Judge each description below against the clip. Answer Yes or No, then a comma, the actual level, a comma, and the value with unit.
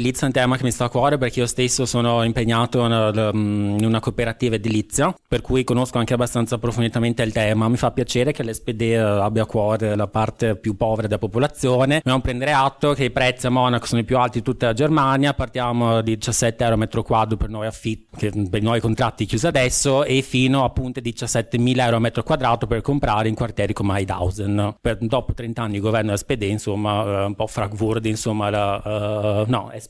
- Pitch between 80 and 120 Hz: Yes, low, 115 Hz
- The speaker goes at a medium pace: No, fast, 200 wpm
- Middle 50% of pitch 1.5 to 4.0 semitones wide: Yes, narrow, 2.5 semitones